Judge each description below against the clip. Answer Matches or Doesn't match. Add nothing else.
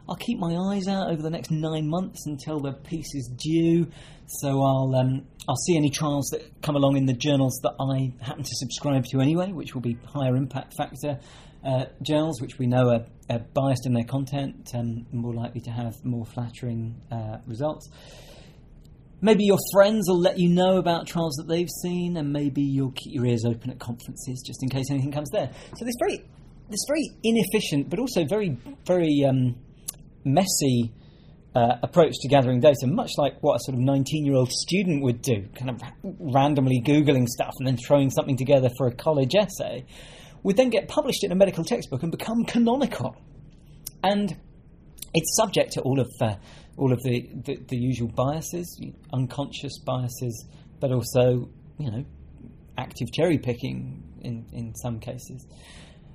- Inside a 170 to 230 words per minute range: Matches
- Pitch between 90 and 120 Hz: Doesn't match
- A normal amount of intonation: Matches